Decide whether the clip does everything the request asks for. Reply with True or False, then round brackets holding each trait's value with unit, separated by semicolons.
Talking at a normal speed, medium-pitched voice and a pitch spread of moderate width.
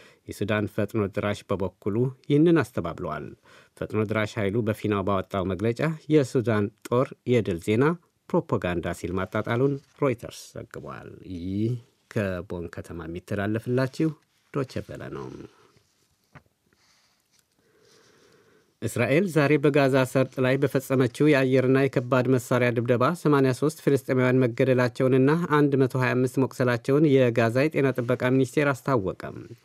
False (95 wpm; 125 Hz; 4.3 semitones)